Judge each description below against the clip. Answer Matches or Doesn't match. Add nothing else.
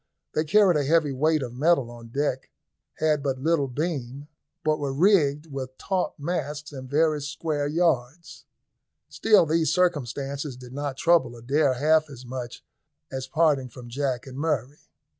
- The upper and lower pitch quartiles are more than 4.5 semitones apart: Doesn't match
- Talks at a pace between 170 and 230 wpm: Doesn't match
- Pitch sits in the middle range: Matches